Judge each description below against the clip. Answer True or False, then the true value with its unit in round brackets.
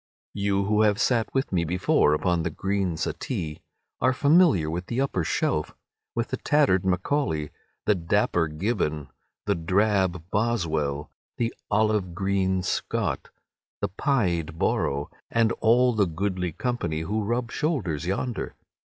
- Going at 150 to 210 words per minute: False (135 wpm)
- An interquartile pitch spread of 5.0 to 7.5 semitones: True (5.5 semitones)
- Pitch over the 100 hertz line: False (95 Hz)